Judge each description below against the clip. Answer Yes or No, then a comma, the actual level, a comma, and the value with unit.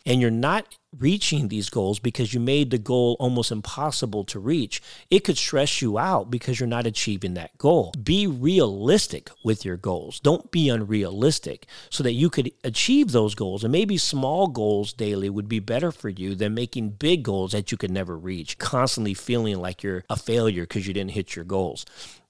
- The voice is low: Yes, low, 115 Hz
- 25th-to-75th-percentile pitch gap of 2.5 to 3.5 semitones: No, average, 5.1 semitones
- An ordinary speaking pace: Yes, average, 195 wpm